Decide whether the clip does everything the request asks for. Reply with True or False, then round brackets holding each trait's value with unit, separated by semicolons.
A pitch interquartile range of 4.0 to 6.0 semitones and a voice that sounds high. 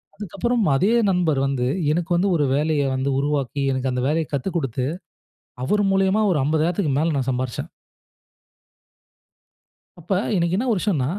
False (4.9 semitones; 155 Hz)